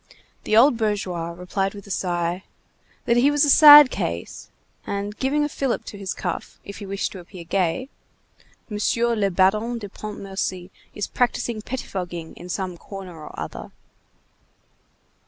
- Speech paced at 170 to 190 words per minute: No, average, 155 wpm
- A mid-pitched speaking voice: No, high, 200 Hz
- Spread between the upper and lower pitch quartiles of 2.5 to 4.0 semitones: No, average, 4.4 semitones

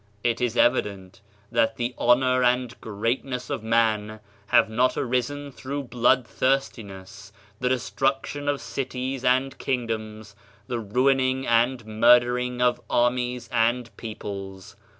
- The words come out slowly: Yes, slow, 120 wpm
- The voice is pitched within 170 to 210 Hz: No, low, 120 Hz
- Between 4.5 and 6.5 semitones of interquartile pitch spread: No, narrow, 2.4 semitones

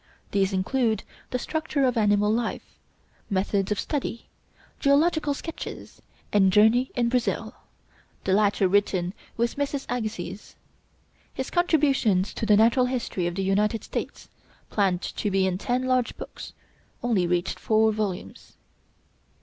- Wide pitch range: No, average, 4.6 semitones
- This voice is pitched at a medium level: No, high, 220 Hz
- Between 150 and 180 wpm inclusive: No, slow, 135 wpm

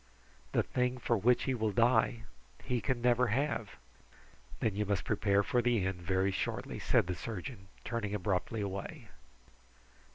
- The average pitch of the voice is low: Yes, low, 110 Hz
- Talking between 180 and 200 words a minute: No, average, 155 wpm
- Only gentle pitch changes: No, average, 3.7 semitones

